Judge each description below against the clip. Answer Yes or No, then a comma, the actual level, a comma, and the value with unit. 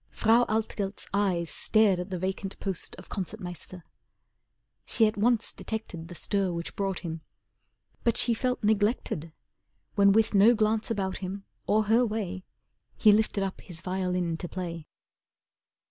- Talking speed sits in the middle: Yes, average, 150 wpm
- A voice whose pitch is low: No, high, 195 Hz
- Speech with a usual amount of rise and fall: Yes, average, 3.1 semitones